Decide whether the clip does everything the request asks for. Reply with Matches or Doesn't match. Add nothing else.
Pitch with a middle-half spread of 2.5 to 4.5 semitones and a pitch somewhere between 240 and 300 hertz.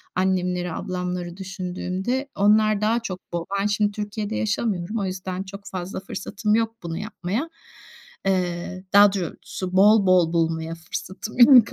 Doesn't match